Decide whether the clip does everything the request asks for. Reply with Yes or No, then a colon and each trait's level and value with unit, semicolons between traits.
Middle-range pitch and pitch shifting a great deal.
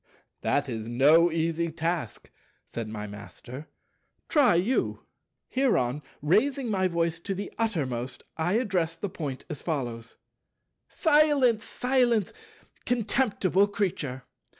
Yes: medium, 170 Hz; wide, 8.5 semitones